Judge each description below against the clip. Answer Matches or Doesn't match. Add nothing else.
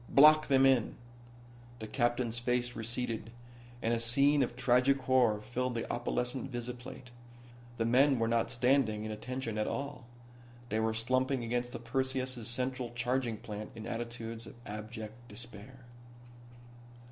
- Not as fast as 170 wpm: Matches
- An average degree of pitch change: Doesn't match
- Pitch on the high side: Doesn't match